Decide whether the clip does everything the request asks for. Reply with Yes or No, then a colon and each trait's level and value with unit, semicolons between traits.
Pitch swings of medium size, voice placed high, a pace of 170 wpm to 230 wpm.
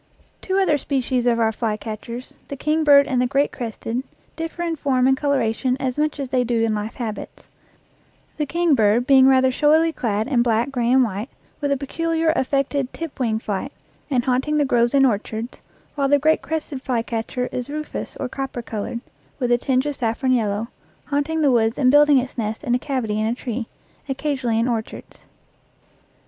Yes: average, 3.5 semitones; very high, 255 Hz; average, 190 wpm